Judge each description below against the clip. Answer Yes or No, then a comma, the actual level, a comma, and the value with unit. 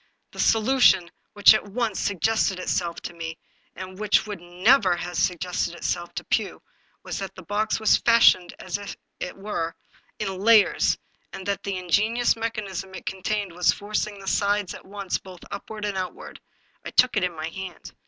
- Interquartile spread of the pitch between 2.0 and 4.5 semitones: Yes, average, 2.9 semitones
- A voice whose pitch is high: Yes, high, 195 Hz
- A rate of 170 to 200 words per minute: Yes, average, 185 wpm